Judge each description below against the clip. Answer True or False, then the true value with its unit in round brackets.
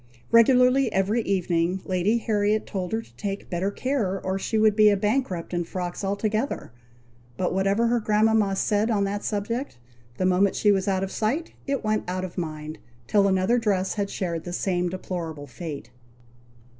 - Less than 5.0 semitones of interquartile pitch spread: True (2.9 semitones)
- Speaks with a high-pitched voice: True (200 Hz)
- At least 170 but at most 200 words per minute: True (175 wpm)